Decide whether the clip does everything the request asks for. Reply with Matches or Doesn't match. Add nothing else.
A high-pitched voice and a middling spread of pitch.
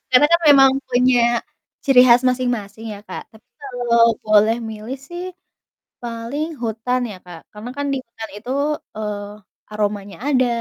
Matches